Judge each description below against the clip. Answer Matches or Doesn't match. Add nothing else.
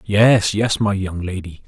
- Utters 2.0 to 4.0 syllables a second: Matches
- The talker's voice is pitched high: Doesn't match